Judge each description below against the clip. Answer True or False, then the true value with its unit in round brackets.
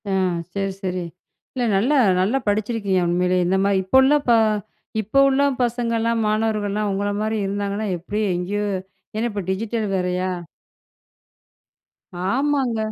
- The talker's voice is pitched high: True (210 Hz)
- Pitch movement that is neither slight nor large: True (3.2 semitones)